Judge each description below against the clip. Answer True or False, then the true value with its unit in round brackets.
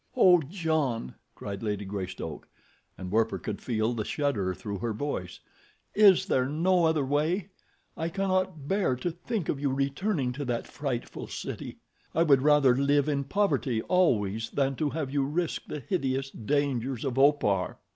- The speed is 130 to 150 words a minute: False (160 wpm)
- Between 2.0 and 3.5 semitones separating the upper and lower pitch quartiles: False (5.6 semitones)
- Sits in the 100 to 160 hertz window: True (140 Hz)